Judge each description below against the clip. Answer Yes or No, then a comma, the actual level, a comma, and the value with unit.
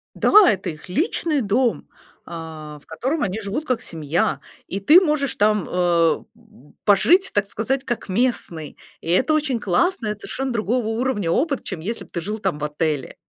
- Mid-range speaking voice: No, high, 210 Hz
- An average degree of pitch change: No, wide, 7.4 semitones